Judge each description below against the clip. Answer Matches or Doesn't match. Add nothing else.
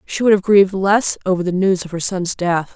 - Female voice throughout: Matches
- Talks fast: Matches